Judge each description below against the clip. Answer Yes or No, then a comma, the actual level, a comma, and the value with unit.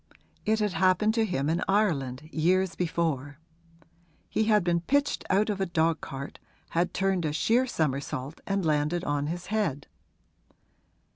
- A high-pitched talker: No, medium, 175 Hz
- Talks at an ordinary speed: Yes, average, 145 wpm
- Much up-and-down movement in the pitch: No, average, 4.8 semitones